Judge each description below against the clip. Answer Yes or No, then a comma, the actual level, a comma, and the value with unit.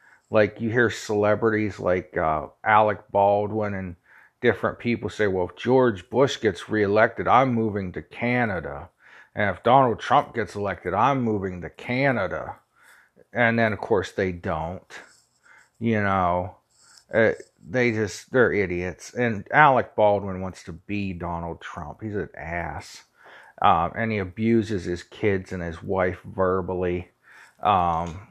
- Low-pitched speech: Yes, low, 105 Hz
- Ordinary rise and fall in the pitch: Yes, average, 3.6 semitones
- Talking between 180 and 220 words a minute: No, average, 140 wpm